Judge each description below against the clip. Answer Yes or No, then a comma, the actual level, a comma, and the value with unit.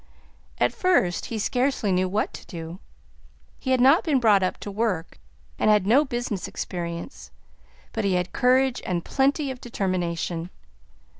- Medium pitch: No, high, 205 Hz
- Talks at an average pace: Yes, average, 155 wpm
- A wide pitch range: Yes, wide, 6.1 semitones